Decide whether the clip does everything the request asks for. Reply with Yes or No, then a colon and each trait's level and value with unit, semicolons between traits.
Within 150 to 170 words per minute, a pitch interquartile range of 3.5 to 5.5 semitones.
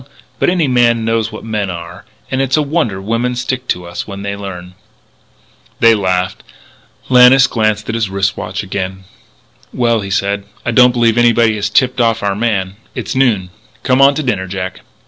No: average, 180 wpm; average, 4.1 semitones